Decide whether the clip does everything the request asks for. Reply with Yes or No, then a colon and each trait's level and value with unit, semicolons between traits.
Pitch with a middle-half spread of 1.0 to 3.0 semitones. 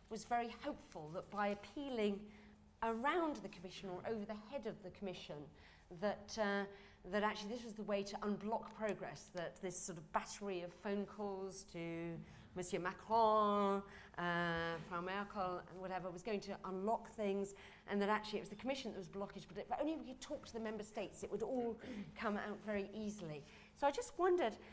Yes: average, 2.7 semitones